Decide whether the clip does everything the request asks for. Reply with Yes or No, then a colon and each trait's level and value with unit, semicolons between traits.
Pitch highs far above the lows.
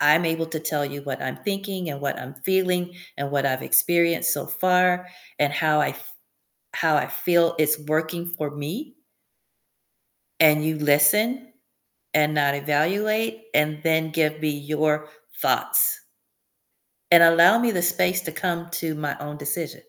No: average, 3.2 semitones